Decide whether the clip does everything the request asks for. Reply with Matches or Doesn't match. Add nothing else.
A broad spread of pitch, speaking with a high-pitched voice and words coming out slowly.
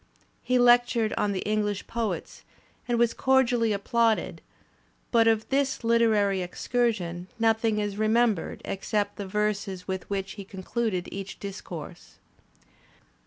Doesn't match